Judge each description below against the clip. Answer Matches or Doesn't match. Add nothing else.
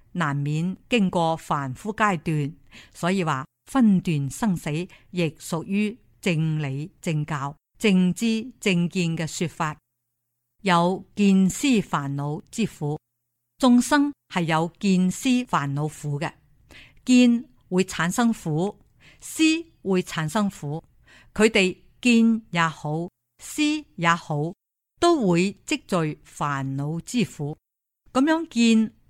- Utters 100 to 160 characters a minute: Matches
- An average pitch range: Doesn't match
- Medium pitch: Matches